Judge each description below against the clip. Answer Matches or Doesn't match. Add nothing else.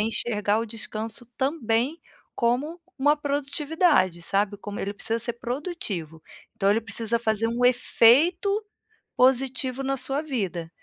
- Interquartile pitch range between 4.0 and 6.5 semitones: Matches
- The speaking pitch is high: Matches